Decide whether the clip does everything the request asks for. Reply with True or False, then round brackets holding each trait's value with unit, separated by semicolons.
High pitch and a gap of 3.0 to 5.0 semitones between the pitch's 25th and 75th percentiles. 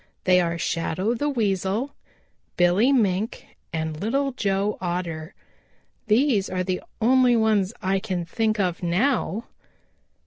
True (195 Hz; 4.2 semitones)